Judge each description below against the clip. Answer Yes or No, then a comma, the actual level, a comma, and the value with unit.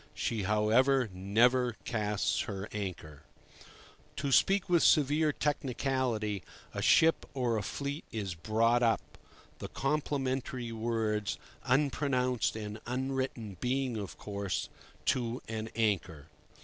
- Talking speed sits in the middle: No, slow, 110 wpm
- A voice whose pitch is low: Yes, low, 115 Hz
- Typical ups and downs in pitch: Yes, average, 4.0 semitones